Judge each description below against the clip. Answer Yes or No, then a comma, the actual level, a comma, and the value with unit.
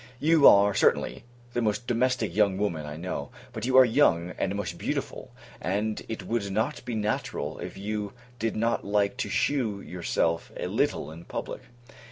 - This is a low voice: Yes, low, 105 Hz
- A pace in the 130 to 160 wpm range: No, average, 175 wpm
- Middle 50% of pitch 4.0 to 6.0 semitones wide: No, average, 3.4 semitones